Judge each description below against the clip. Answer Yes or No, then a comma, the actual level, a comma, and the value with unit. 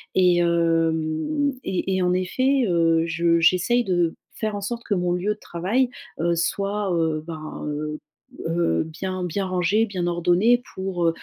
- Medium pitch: Yes, medium, 180 Hz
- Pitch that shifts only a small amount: No, average, 3.2 semitones